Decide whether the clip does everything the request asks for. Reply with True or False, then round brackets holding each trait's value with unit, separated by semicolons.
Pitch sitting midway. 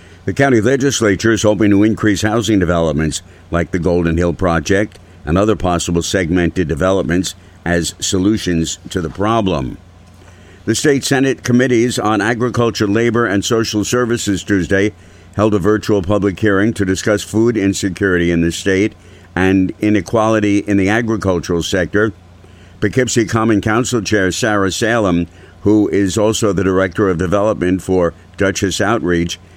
False (100 Hz)